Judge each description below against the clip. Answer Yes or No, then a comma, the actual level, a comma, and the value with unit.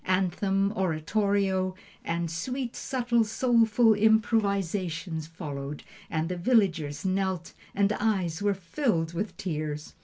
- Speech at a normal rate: No, slow, 110 wpm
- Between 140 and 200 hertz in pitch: Yes, high, 190 Hz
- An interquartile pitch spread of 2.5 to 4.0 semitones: No, average, 4.4 semitones